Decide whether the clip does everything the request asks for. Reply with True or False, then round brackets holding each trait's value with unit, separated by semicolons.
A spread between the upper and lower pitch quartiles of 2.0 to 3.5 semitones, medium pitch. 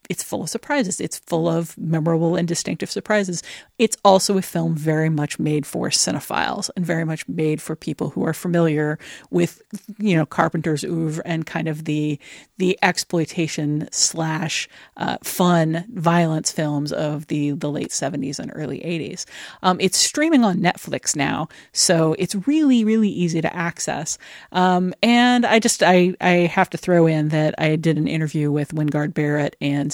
True (2.9 semitones; 165 Hz)